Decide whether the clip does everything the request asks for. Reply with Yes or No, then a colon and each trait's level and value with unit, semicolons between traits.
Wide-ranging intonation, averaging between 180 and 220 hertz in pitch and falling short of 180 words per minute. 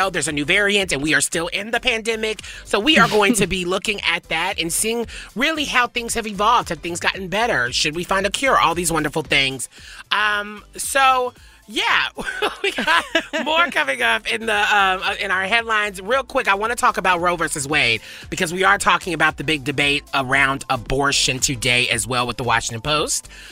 No: wide, 6.6 semitones; high, 190 Hz; fast, 205 wpm